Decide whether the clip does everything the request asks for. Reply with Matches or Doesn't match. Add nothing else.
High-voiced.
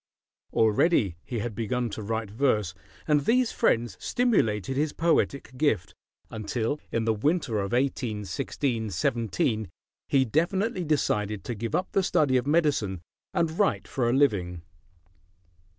Doesn't match